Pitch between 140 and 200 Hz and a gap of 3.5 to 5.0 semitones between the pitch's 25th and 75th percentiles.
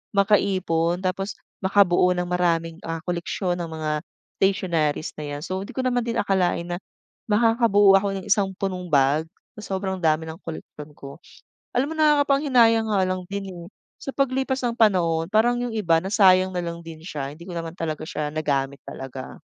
Yes: medium, 185 Hz; average, 3.9 semitones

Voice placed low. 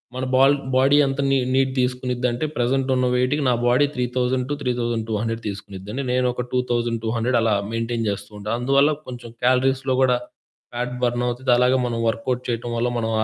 Yes: low, 125 Hz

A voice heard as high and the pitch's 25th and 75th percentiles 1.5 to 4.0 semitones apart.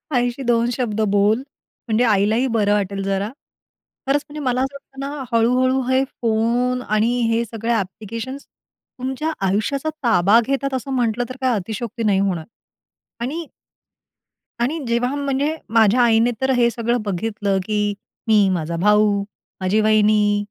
Yes: high, 230 Hz; average, 3.6 semitones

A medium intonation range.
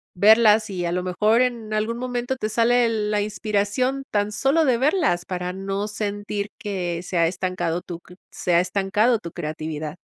Yes: average, 4.2 semitones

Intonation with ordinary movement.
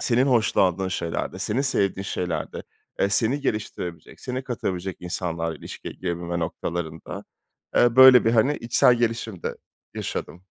No: wide, 5.7 semitones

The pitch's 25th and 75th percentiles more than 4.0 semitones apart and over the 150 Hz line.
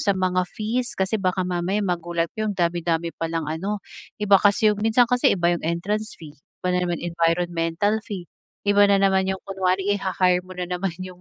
No: average, 2.8 semitones; medium, 185 Hz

